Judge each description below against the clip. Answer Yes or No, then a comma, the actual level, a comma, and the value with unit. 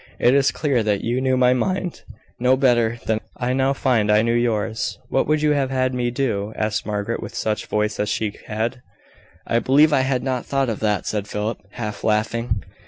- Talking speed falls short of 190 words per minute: No, fast, 205 wpm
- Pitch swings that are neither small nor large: Yes, average, 3.5 semitones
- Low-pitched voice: Yes, low, 120 Hz